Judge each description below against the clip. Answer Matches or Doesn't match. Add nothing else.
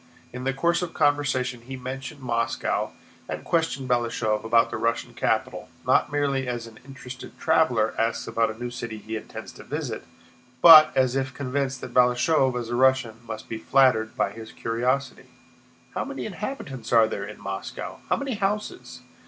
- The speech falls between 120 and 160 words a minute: Doesn't match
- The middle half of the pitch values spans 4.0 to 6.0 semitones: Doesn't match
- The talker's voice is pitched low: Matches